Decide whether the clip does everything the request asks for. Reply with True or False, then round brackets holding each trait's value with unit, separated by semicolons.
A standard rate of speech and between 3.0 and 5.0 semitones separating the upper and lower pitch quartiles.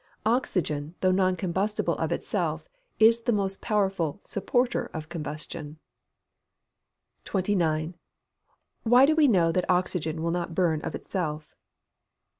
False (120 wpm; 4.4 semitones)